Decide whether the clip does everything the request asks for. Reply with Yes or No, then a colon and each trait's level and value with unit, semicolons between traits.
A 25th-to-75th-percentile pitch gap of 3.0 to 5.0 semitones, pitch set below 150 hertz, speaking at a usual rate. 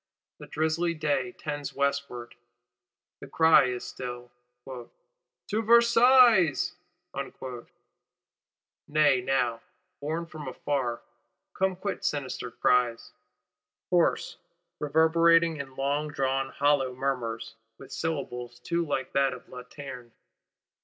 No: average, 4.2 semitones; medium, 140 Hz; slow, 95 wpm